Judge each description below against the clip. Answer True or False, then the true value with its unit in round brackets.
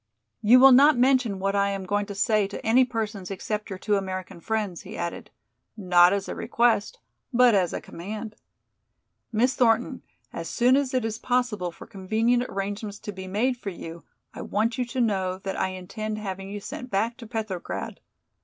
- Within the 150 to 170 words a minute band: False (190 wpm)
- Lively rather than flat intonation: False (3.6 semitones)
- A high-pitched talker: True (210 Hz)